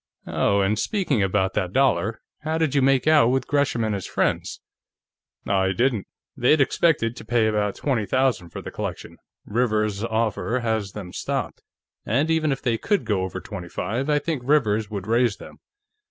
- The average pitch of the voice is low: Yes, low, 115 Hz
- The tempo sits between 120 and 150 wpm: No, average, 180 wpm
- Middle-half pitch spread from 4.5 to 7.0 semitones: Yes, average, 4.9 semitones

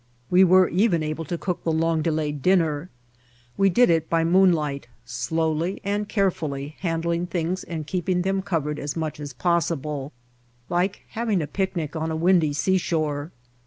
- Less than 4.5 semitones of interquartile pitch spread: Yes, average, 3.3 semitones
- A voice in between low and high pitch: Yes, medium, 165 Hz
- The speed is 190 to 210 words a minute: No, average, 160 wpm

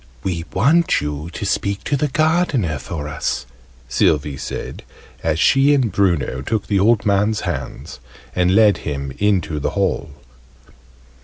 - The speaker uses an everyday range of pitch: No, wide, 6.8 semitones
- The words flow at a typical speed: Yes, average, 145 wpm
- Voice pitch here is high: No, very low, 95 Hz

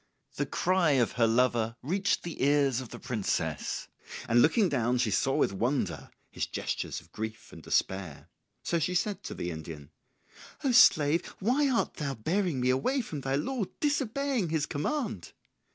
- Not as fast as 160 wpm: No, average, 170 wpm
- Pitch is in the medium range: Yes, medium, 145 Hz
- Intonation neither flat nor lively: No, wide, 9.0 semitones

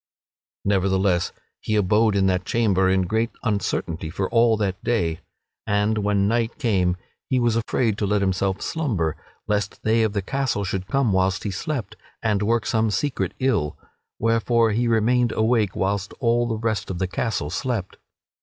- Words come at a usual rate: Yes, average, 170 wpm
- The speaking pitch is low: Yes, low, 105 Hz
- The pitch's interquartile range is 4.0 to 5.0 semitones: No, average, 3.3 semitones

